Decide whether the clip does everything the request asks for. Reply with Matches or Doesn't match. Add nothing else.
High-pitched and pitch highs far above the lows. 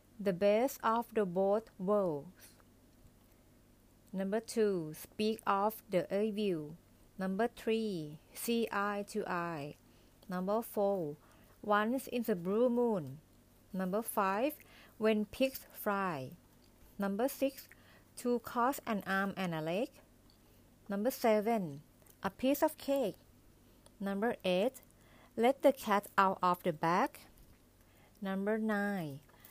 Doesn't match